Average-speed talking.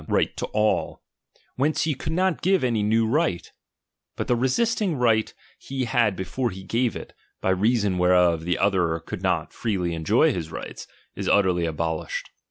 Yes: average, 175 wpm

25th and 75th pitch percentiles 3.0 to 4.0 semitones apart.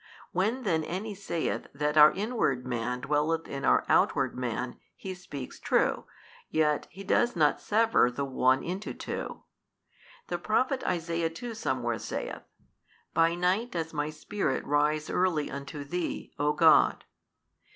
No: average, 4.9 semitones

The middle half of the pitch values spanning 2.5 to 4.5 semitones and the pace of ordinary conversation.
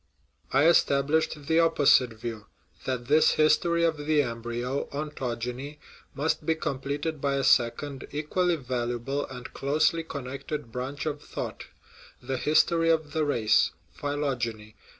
No: average, 3.6 semitones; slow, 130 wpm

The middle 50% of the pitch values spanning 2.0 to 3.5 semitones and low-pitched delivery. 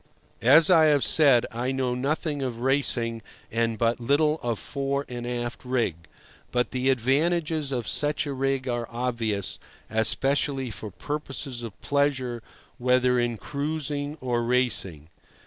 Yes: average, 3.1 semitones; low, 130 Hz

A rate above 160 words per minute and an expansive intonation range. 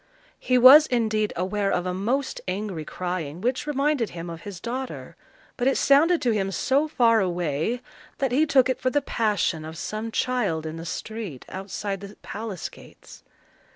Yes: average, 175 wpm; wide, 5.9 semitones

